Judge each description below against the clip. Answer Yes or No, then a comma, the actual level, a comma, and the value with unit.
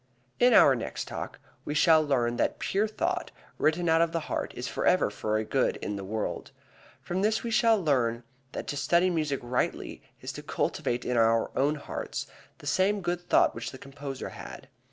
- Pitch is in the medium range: Yes, medium, 150 Hz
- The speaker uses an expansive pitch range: Yes, wide, 6.3 semitones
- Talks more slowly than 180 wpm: No, average, 190 wpm